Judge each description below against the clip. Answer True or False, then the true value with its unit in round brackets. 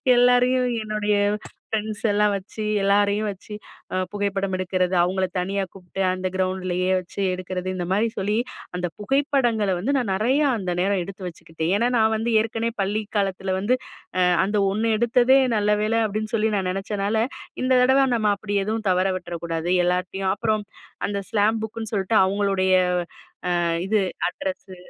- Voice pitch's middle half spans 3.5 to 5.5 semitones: False (2.8 semitones)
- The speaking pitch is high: True (205 Hz)